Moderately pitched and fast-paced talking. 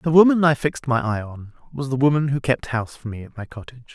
No: low, 130 Hz; fast, 275 wpm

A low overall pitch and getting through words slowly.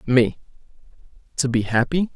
Yes: low, 130 Hz; slow, 110 wpm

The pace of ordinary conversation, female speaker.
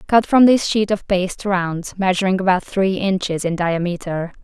Yes: average, 175 wpm; female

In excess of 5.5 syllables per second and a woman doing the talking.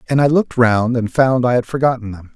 No: 6.0 syllables/s; male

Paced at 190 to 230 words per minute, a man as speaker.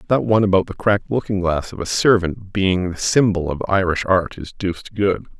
Yes: average, 200 wpm; male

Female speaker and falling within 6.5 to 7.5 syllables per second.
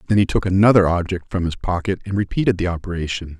No: male; 6.7 syllables/s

